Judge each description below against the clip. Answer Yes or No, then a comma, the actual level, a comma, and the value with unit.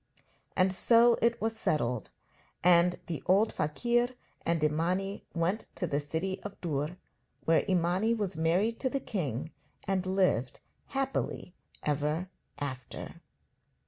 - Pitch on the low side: No, medium, 180 Hz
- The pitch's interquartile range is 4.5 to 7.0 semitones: Yes, average, 5.1 semitones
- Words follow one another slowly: Yes, slow, 125 wpm